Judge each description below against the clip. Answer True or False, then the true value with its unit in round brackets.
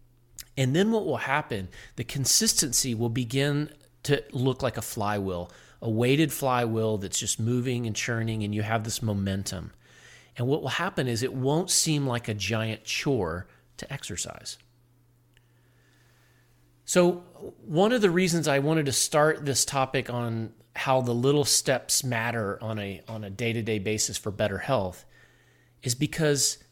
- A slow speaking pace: False (160 wpm)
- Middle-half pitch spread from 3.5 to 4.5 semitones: True (4.0 semitones)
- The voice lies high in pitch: False (120 Hz)